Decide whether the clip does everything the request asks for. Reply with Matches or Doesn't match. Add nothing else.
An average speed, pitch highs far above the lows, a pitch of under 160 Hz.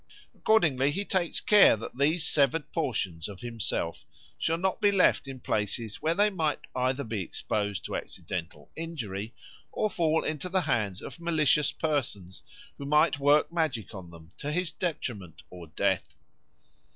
Matches